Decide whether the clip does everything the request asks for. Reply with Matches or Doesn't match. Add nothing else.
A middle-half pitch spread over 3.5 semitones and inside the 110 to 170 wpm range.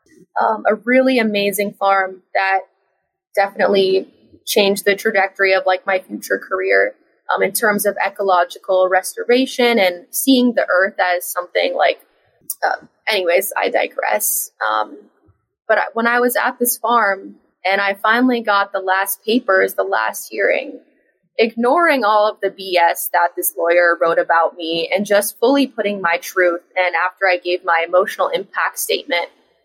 Doesn't match